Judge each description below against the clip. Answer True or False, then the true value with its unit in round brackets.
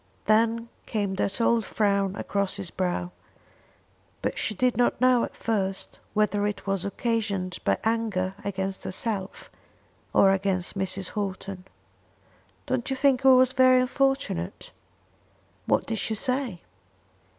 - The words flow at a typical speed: False (130 wpm)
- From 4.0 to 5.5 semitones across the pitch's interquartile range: False (3.5 semitones)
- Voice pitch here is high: True (205 Hz)